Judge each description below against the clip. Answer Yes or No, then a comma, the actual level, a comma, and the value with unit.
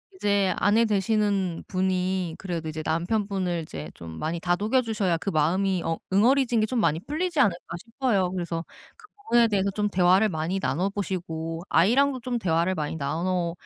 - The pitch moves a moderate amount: Yes, average, 4.2 semitones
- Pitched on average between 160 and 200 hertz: Yes, medium, 185 Hz